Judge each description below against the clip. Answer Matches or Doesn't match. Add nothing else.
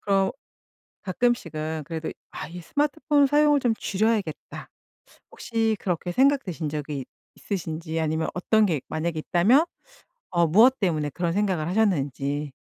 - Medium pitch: Matches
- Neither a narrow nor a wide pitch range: Doesn't match